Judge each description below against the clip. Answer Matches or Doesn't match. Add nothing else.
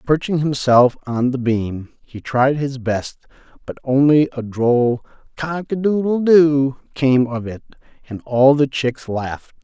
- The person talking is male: Matches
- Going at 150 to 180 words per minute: Matches